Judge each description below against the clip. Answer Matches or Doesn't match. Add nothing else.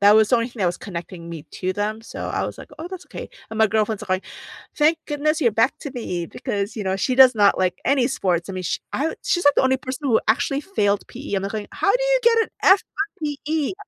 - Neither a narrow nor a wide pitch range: Doesn't match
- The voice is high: Matches